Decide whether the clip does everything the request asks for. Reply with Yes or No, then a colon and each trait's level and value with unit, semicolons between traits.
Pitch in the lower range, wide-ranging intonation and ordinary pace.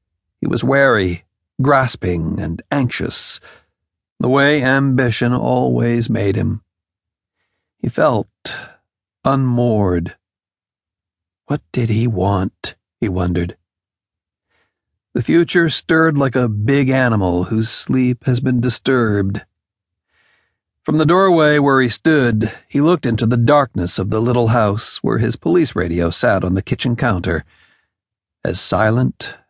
No: low, 110 Hz; wide, 5.8 semitones; slow, 120 wpm